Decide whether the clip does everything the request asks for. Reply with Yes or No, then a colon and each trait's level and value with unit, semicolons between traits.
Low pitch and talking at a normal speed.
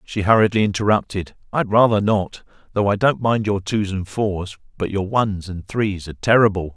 Yes: low, 100 Hz; average, 185 wpm